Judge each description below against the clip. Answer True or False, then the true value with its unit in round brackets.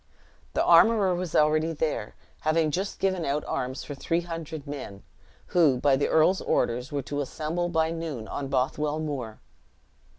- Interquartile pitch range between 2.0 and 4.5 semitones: True (3.0 semitones)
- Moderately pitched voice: True (155 Hz)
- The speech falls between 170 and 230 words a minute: False (160 wpm)